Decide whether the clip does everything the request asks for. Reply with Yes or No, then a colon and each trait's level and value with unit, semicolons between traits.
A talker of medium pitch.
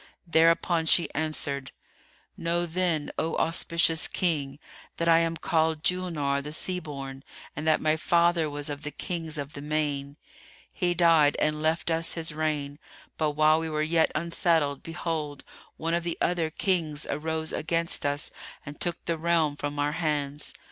Yes: medium, 160 Hz